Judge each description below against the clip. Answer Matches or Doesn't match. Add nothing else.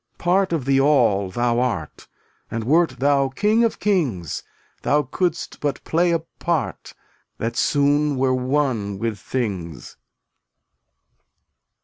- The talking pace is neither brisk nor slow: Doesn't match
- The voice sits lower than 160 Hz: Matches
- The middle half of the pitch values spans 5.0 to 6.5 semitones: Matches